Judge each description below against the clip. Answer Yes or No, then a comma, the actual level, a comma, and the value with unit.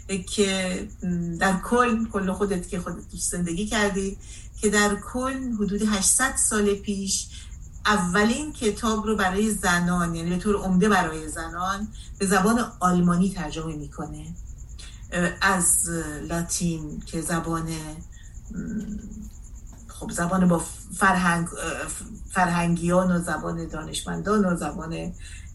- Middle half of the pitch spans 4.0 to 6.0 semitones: No, average, 3.6 semitones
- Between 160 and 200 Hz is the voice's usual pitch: Yes, medium, 185 Hz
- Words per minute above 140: No, slow, 105 wpm